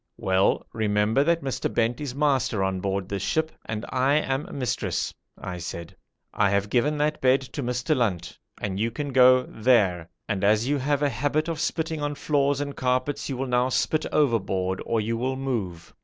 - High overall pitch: No, low, 125 Hz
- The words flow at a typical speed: Yes, average, 190 wpm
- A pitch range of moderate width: No, wide, 5.7 semitones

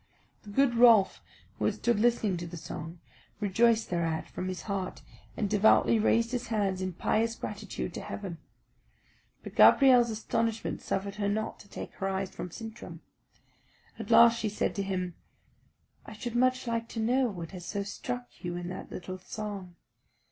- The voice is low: No, high, 205 Hz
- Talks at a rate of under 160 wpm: No, average, 170 wpm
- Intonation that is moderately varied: Yes, average, 3.7 semitones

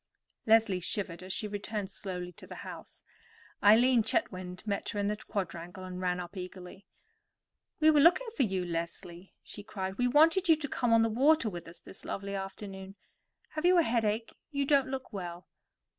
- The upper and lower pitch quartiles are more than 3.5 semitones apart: Yes, average, 5.1 semitones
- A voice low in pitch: No, high, 205 Hz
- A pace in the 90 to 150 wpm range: No, average, 185 wpm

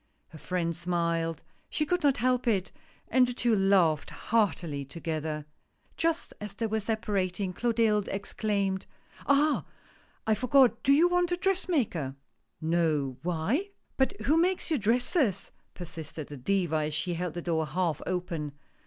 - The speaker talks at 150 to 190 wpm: Yes, average, 165 wpm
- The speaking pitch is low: No, high, 195 Hz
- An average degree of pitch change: No, wide, 7.2 semitones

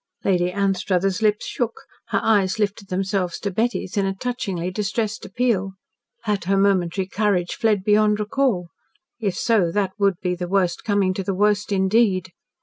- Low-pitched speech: No, high, 195 Hz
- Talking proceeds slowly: No, average, 160 wpm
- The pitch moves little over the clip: Yes, narrow, 2.1 semitones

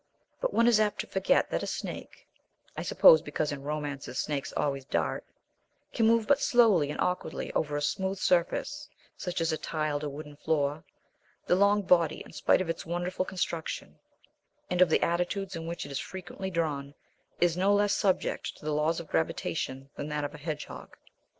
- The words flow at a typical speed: Yes, average, 190 wpm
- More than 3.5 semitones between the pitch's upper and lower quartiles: Yes, average, 4.2 semitones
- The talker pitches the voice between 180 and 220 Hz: No, medium, 165 Hz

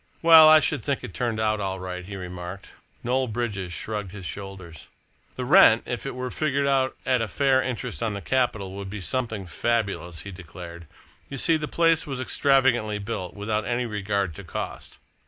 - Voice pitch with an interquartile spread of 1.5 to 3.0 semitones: No, average, 5.1 semitones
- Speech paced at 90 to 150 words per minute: No, average, 190 wpm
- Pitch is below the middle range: Yes, low, 110 Hz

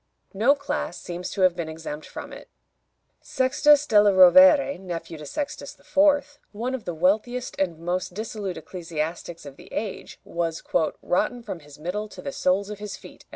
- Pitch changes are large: Yes, wide, 6.1 semitones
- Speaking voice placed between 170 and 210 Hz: Yes, high, 190 Hz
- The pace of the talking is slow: No, average, 170 wpm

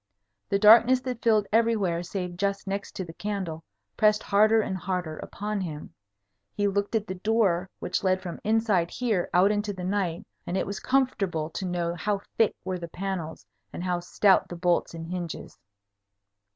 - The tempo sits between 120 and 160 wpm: No, average, 180 wpm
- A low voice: No, high, 195 Hz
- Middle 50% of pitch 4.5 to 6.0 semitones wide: No, average, 3.2 semitones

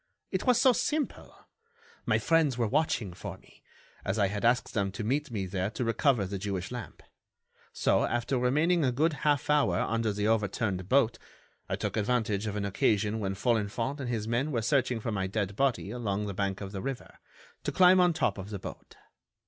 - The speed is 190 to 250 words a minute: Yes, average, 200 wpm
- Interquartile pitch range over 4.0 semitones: Yes, average, 5.1 semitones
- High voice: No, low, 115 Hz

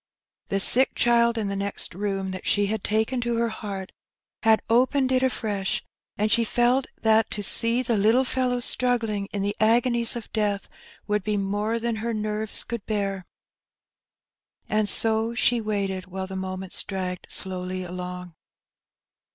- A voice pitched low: No, high, 215 Hz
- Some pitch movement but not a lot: Yes, average, 3.1 semitones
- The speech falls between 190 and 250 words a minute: No, average, 160 wpm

